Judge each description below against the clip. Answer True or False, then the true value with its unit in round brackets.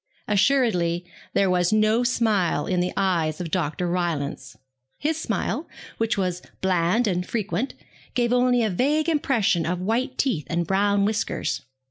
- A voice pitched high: True (195 Hz)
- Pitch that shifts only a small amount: False (5.3 semitones)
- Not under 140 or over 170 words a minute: True (145 wpm)